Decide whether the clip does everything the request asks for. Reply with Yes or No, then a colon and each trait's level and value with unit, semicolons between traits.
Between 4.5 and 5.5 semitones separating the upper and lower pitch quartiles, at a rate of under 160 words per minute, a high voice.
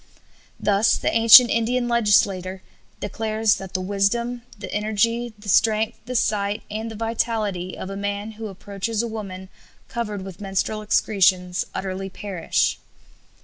No: narrow, 2.6 semitones; average, 140 wpm; high, 210 Hz